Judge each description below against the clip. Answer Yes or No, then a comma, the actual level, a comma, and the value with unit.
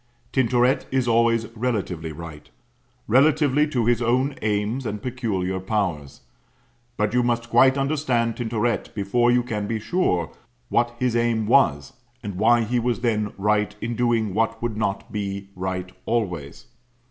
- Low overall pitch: Yes, low, 115 Hz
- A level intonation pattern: No, average, 3.1 semitones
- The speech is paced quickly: No, average, 145 wpm